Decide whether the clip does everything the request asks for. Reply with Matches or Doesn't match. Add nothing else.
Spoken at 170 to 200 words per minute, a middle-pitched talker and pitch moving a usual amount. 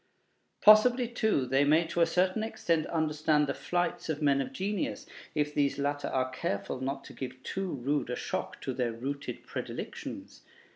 Matches